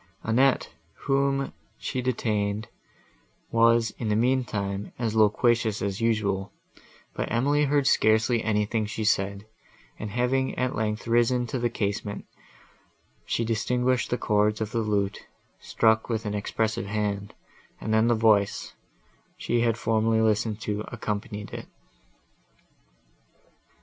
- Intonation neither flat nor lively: No, narrow, 2.3 semitones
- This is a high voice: No, low, 110 Hz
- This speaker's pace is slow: Yes, slow, 125 wpm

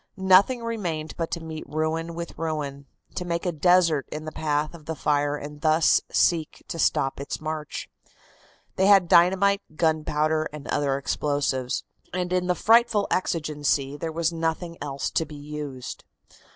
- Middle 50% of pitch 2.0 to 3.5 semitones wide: Yes, average, 2.9 semitones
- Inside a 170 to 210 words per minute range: No, average, 160 wpm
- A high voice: No, medium, 160 Hz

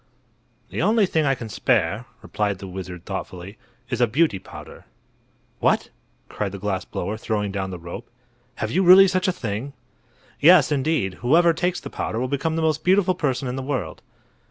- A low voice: Yes, low, 125 Hz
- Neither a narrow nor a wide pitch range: No, wide, 8.3 semitones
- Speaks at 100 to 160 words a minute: No, average, 180 wpm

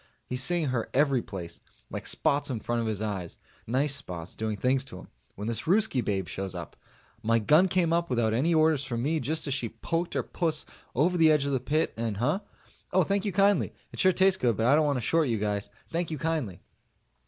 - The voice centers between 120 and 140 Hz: Yes, low, 135 Hz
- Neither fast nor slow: No, fast, 230 wpm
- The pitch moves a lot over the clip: Yes, wide, 6.3 semitones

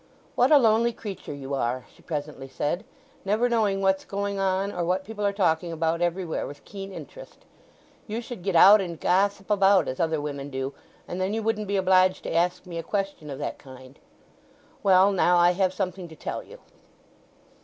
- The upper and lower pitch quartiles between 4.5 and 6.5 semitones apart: No, average, 3.6 semitones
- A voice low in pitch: No, medium, 185 Hz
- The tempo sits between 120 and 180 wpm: No, average, 195 wpm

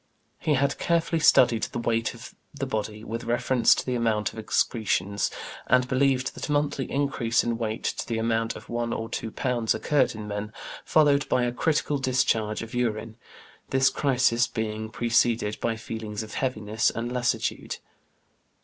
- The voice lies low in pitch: Yes, low, 115 Hz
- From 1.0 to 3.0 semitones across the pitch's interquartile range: Yes, average, 2.7 semitones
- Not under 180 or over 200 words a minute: No, average, 165 wpm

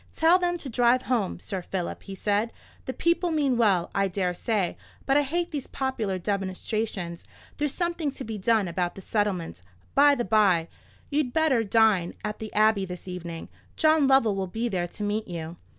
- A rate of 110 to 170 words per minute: No, average, 185 wpm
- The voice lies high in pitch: Yes, high, 215 Hz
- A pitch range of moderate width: No, wide, 6.2 semitones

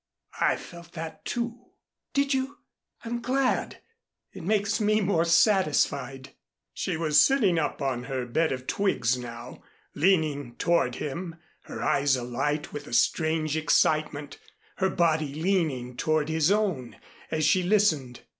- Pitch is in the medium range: Yes, medium, 160 Hz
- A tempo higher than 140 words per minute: No, slow, 135 wpm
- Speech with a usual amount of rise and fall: No, wide, 5.8 semitones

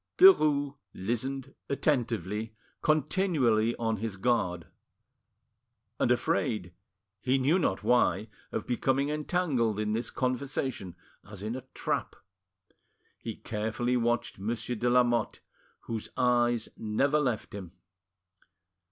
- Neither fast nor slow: No, slow, 110 wpm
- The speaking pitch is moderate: No, low, 120 Hz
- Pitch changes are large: No, average, 3.8 semitones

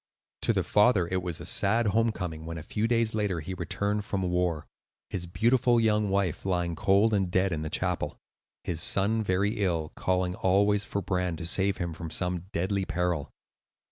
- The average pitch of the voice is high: No, very low, 95 Hz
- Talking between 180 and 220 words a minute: Yes, average, 185 wpm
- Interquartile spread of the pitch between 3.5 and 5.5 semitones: No, average, 2.9 semitones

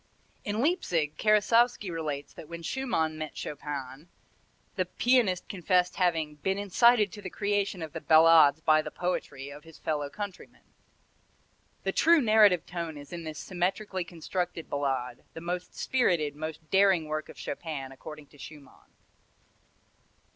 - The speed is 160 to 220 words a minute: No, average, 145 wpm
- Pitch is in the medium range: Yes, medium, 170 Hz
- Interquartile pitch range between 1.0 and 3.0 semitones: No, average, 4.5 semitones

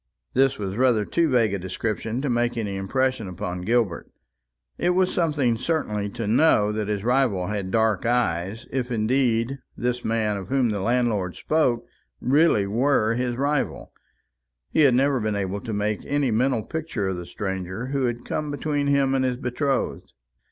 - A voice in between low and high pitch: No, low, 120 Hz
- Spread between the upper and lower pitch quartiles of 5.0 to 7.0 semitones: No, average, 4.5 semitones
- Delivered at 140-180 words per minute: Yes, average, 175 wpm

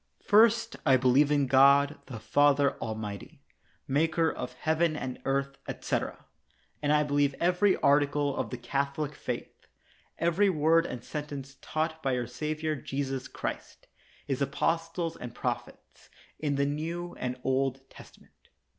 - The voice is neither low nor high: Yes, medium, 145 Hz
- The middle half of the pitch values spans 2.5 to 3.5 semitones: Yes, average, 2.9 semitones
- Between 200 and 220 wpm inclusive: No, slow, 135 wpm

